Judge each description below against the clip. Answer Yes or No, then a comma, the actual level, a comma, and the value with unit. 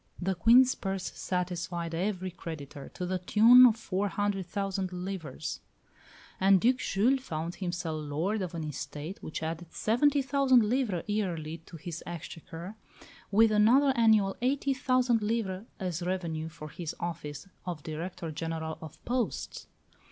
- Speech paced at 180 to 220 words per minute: No, average, 145 wpm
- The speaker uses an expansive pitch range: No, average, 4.9 semitones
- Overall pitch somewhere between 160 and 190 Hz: Yes, medium, 185 Hz